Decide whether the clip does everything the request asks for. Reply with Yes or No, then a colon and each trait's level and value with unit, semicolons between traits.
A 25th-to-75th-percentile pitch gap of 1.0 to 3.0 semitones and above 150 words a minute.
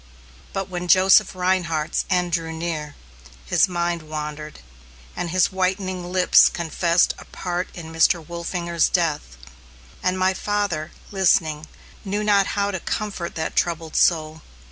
No: narrow, 2.6 semitones; slow, 135 wpm